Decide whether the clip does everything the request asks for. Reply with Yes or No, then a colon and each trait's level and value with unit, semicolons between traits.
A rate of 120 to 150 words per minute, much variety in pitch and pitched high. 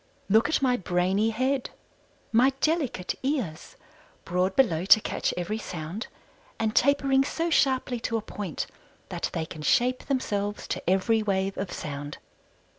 Yes: average, 145 wpm; wide, 6.1 semitones; high, 215 Hz